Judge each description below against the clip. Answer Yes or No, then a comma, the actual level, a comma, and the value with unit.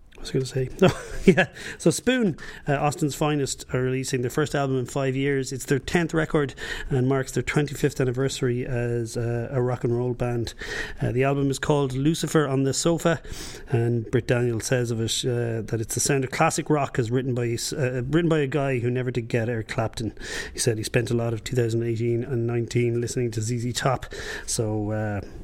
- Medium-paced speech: No, fast, 210 wpm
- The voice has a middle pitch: No, low, 125 Hz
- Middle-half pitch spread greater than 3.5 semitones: No, average, 2.8 semitones